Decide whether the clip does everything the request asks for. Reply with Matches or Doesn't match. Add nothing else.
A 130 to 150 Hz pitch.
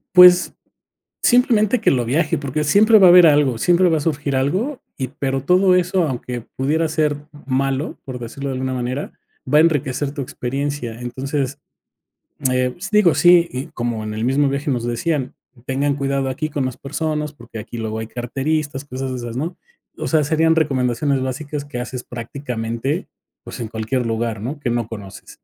Matches